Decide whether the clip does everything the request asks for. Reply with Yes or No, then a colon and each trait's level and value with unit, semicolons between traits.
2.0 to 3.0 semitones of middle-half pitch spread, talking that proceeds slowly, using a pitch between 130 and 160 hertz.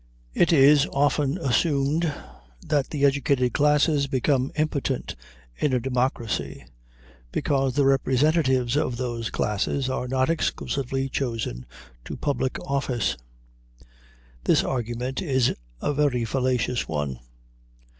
Yes: narrow, 2.5 semitones; slow, 110 wpm; low, 135 Hz